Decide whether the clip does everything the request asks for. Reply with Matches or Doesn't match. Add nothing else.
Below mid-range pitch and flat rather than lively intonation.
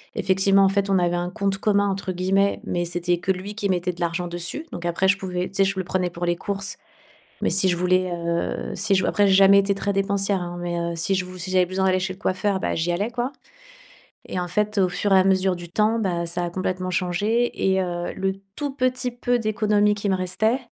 Doesn't match